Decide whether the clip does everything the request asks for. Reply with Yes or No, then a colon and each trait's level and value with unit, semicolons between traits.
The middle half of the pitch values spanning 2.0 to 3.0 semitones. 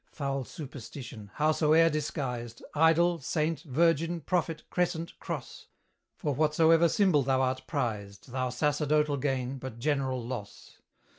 No: average, 3.9 semitones